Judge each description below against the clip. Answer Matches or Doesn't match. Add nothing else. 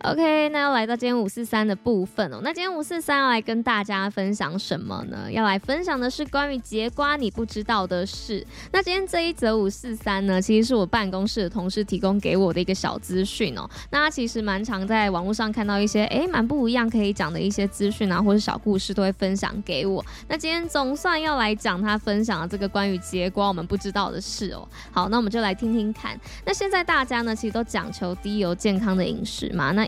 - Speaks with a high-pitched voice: Matches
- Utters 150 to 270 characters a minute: Doesn't match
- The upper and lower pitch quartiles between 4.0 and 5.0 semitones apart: Doesn't match